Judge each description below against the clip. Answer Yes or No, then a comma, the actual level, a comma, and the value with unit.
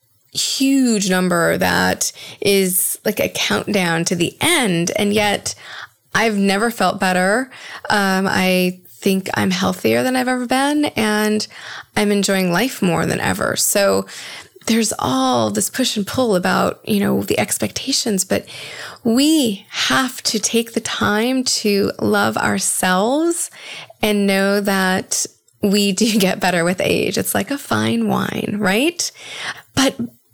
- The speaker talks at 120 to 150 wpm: Yes, average, 140 wpm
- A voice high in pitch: Yes, high, 205 Hz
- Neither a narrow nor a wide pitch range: Yes, average, 3.8 semitones